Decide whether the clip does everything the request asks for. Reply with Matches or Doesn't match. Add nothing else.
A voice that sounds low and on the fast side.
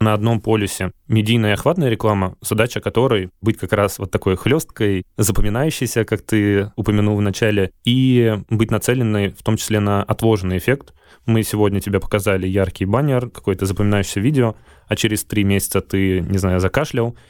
Matches